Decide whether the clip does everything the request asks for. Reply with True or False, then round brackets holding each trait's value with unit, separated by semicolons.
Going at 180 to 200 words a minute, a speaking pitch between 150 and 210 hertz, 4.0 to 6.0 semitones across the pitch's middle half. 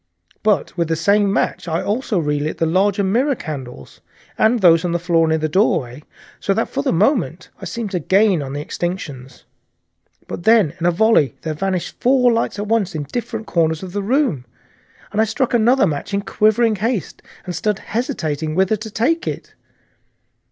True (190 wpm; 190 Hz; 5.4 semitones)